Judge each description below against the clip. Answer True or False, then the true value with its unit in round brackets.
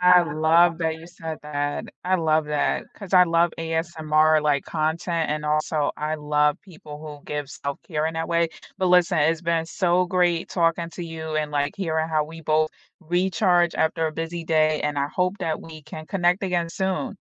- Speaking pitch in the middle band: True (160 Hz)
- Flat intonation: True (2.1 semitones)